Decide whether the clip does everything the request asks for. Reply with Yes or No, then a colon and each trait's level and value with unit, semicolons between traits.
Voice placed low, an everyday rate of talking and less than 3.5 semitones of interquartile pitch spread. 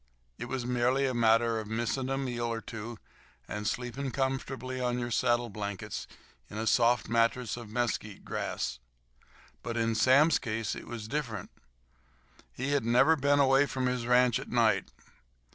Yes: low, 120 Hz; average, 160 wpm; narrow, 2.4 semitones